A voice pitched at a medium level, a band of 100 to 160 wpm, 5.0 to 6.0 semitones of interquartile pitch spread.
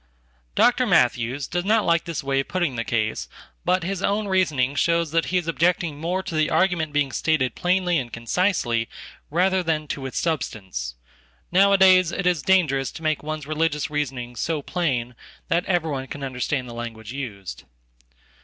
Yes: medium, 155 Hz; average, 155 wpm; wide, 5.4 semitones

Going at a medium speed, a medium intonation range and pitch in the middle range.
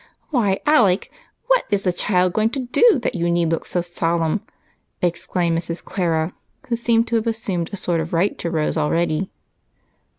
Yes: average, 175 wpm; average, 4.8 semitones; medium, 180 Hz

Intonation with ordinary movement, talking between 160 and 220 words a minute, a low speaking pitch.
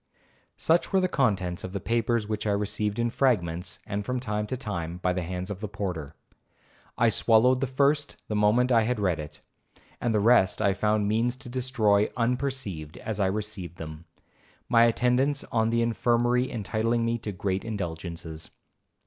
Yes: average, 4.2 semitones; average, 175 wpm; low, 110 Hz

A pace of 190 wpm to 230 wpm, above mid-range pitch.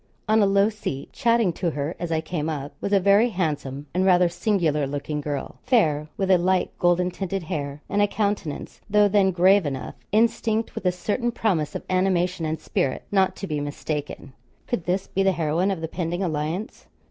No: average, 195 wpm; medium, 180 Hz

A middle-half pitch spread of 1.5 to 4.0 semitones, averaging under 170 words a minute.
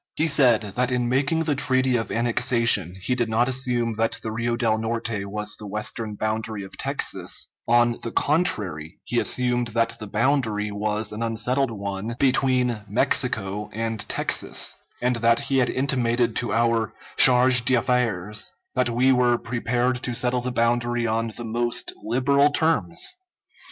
Yes: narrow, 2.4 semitones; average, 155 wpm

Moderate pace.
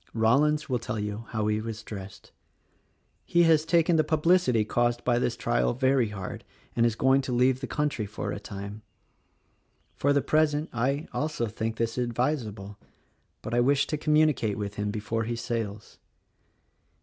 Yes: average, 165 wpm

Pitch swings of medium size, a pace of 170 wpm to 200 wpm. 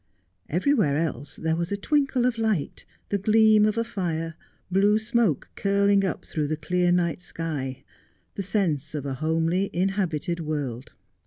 No: average, 4.7 semitones; average, 155 wpm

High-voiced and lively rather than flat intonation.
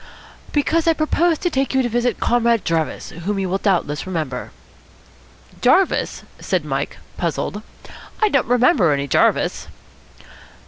Yes: high, 235 Hz; wide, 8.6 semitones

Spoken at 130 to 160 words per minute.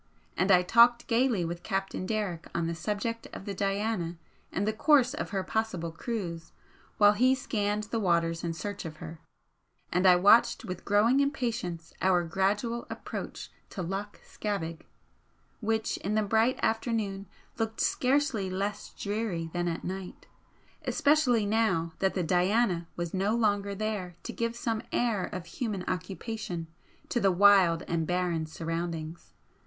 Yes: average, 150 wpm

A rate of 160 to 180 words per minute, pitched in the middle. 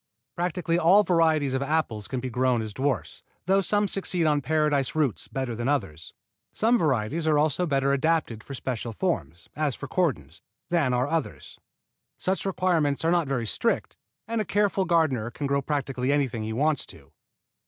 Yes: average, 175 wpm; medium, 145 Hz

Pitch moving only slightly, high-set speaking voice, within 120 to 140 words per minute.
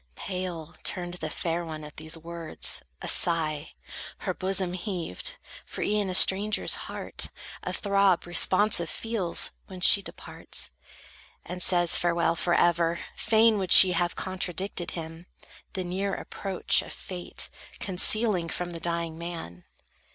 No: narrow, 2.3 semitones; medium, 175 Hz; slow, 135 wpm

